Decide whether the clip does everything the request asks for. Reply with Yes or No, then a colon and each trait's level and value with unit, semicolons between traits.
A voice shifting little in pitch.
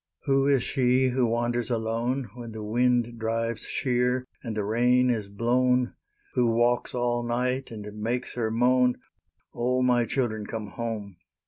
Yes: narrow, 1.7 semitones